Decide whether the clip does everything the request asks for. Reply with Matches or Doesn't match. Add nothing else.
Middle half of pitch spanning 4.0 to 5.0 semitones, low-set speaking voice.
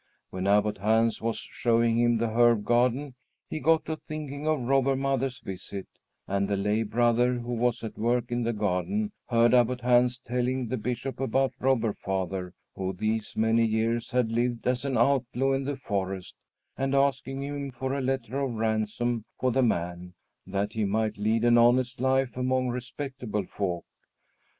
Doesn't match